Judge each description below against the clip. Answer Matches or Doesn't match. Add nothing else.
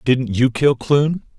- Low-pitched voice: Matches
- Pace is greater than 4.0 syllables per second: Doesn't match